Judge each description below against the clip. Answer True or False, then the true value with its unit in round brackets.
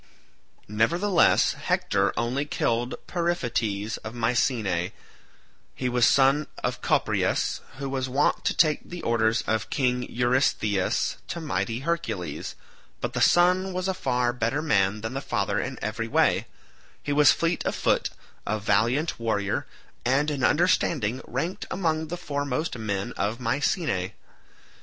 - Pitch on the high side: False (125 Hz)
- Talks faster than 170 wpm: False (140 wpm)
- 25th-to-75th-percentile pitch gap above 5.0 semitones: True (5.5 semitones)